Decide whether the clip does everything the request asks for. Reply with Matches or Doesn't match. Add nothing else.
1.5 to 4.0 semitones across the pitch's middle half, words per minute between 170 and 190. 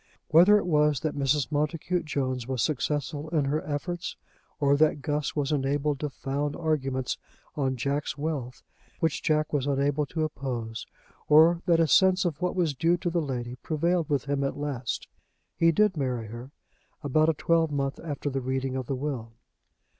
Matches